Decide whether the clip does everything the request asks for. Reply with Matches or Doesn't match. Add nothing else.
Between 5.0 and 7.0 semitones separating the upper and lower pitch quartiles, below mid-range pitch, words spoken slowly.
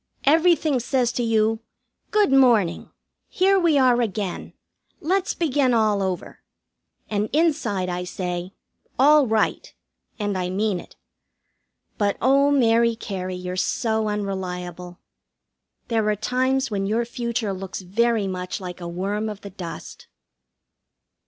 Doesn't match